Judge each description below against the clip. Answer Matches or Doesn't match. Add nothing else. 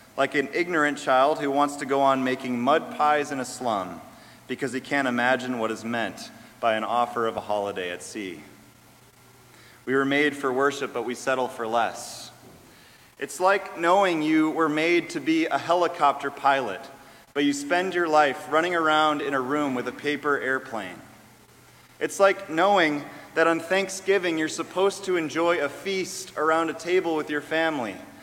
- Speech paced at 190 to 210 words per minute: Doesn't match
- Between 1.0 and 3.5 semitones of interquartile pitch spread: Doesn't match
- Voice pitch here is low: Doesn't match